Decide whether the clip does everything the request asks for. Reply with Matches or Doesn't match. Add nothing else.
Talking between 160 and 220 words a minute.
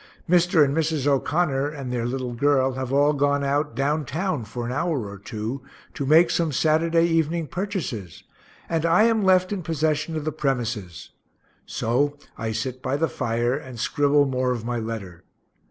Matches